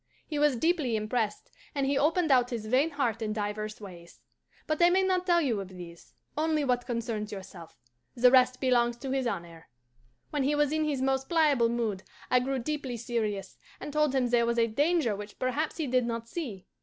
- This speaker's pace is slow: No, fast, 205 wpm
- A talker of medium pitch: No, very high, 250 Hz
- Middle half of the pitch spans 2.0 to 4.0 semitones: No, average, 5.1 semitones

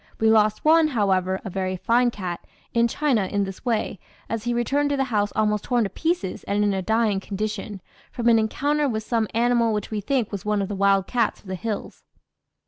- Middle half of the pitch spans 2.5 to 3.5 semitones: Yes, average, 3.2 semitones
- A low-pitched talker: No, high, 215 Hz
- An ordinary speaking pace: No, fast, 220 wpm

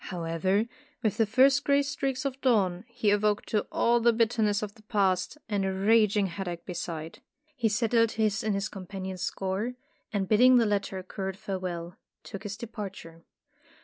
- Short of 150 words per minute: No, average, 170 wpm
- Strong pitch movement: No, average, 3.3 semitones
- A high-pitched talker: Yes, high, 205 Hz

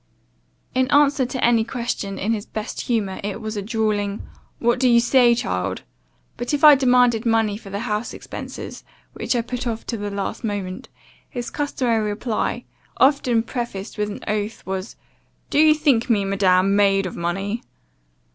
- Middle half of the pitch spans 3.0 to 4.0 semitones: Yes, average, 3.3 semitones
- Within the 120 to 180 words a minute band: Yes, average, 170 wpm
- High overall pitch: Yes, high, 225 Hz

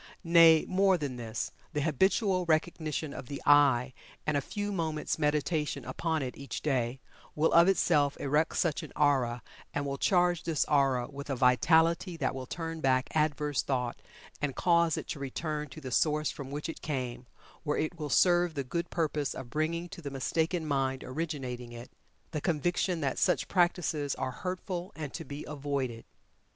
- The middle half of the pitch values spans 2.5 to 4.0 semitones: Yes, average, 3.6 semitones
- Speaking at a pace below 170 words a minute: No, average, 175 wpm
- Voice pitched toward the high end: No, medium, 150 Hz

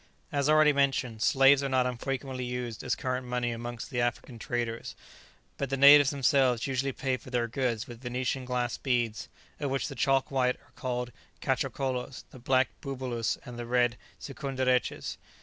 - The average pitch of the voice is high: No, low, 130 Hz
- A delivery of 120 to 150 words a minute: No, average, 165 wpm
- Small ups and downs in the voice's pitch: Yes, narrow, 1.9 semitones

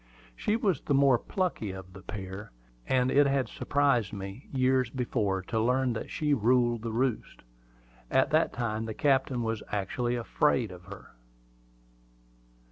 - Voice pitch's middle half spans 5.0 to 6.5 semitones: No, average, 4.0 semitones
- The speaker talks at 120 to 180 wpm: Yes, average, 150 wpm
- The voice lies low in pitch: Yes, low, 120 Hz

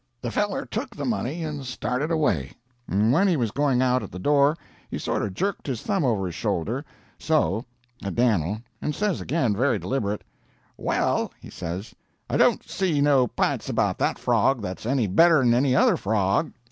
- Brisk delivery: No, average, 180 wpm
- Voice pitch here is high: No, low, 125 Hz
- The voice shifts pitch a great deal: Yes, wide, 6.3 semitones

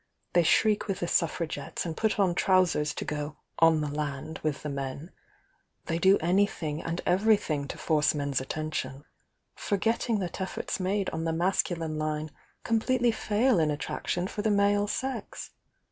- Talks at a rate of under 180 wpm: No, average, 185 wpm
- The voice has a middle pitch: Yes, medium, 170 Hz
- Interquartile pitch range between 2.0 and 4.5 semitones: No, average, 4.9 semitones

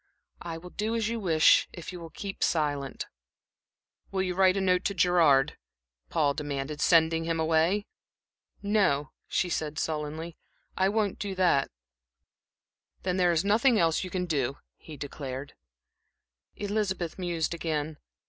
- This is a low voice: No, medium, 170 Hz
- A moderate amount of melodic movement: Yes, average, 3.7 semitones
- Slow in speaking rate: No, average, 145 wpm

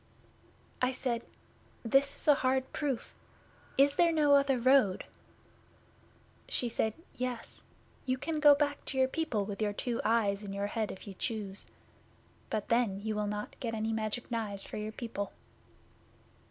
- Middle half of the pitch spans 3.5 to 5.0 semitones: Yes, average, 4.1 semitones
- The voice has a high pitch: Yes, high, 235 Hz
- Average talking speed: Yes, average, 160 wpm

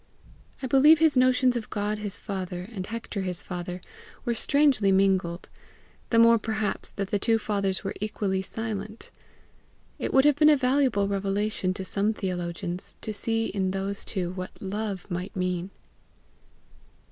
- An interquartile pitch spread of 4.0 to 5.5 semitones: No, average, 3.2 semitones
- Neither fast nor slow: Yes, average, 155 wpm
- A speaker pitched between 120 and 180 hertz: No, high, 200 Hz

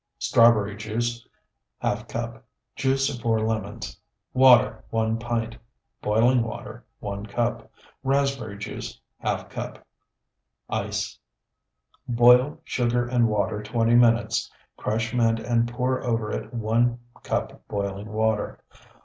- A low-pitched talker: Yes, low, 115 Hz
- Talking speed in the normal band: No, slow, 115 wpm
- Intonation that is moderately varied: No, narrow, 1.8 semitones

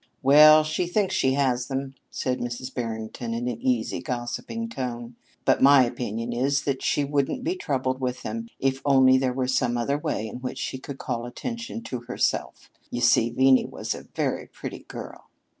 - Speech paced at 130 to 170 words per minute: No, average, 185 wpm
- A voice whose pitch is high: No, low, 130 Hz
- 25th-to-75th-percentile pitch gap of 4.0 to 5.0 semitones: No, narrow, 2.6 semitones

